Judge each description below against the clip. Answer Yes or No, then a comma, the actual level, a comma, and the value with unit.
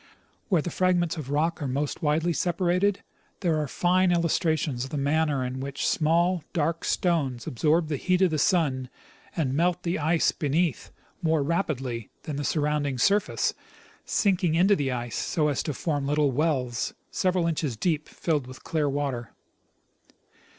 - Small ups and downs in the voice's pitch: No, average, 3.7 semitones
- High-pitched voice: No, medium, 155 Hz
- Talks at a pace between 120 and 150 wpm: No, average, 160 wpm